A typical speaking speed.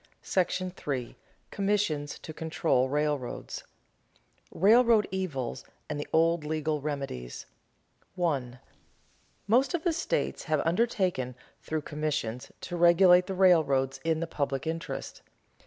No: slow, 120 wpm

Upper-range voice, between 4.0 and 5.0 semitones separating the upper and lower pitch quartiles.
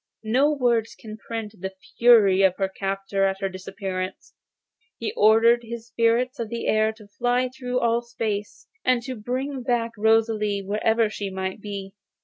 No: high, 220 Hz; average, 3.1 semitones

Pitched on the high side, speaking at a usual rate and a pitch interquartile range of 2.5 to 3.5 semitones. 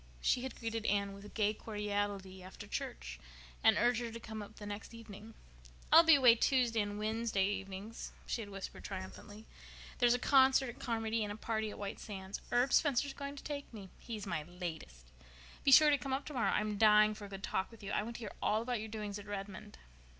No: high, 215 Hz; fast, 215 wpm; average, 2.9 semitones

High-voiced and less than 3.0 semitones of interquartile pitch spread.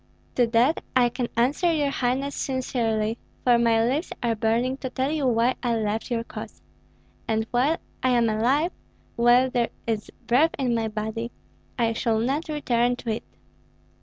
Yes: high, 240 Hz; narrow, 2.4 semitones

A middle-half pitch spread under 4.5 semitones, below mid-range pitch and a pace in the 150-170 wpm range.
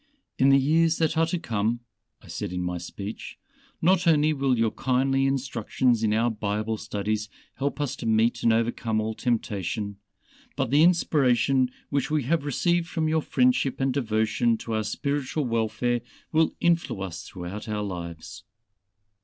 No: average, 5.1 semitones; low, 120 Hz; average, 160 wpm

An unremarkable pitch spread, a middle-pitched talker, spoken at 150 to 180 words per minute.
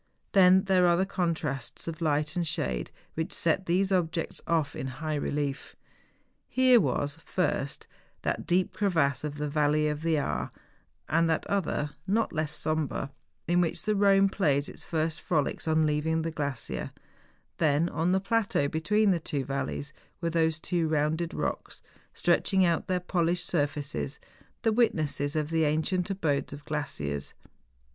Yes: average, 3.5 semitones; medium, 160 Hz; average, 160 wpm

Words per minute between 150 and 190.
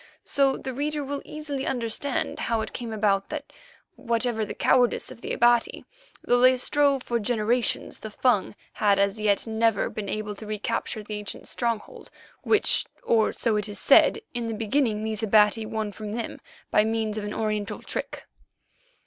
Yes: average, 175 wpm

